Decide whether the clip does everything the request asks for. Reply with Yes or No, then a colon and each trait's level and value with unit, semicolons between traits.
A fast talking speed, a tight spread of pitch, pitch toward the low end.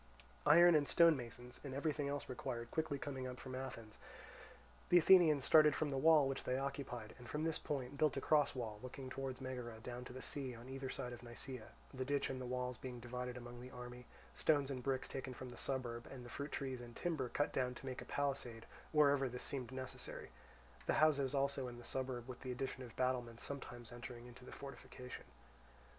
Yes: fast, 210 wpm; narrow, 2.3 semitones; low, 130 Hz